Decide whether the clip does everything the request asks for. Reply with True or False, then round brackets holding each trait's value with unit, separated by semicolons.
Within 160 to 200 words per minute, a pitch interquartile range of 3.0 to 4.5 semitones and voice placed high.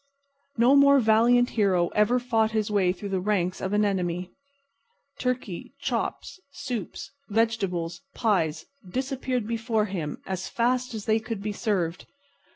False (140 wpm; 4.2 semitones; 215 Hz)